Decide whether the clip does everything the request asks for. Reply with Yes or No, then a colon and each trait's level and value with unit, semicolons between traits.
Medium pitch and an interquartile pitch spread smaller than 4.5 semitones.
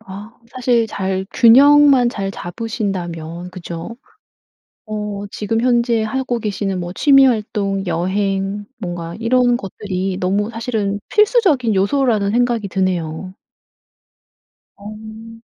No: high, 210 Hz; average, 3.8 semitones